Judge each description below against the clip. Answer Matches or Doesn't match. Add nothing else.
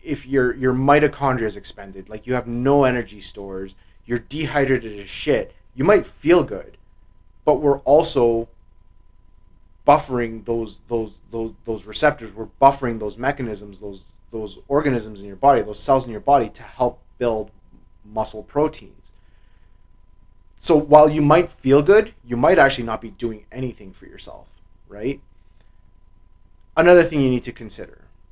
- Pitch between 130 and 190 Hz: Doesn't match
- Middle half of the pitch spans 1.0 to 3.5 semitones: Doesn't match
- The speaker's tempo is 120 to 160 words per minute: Matches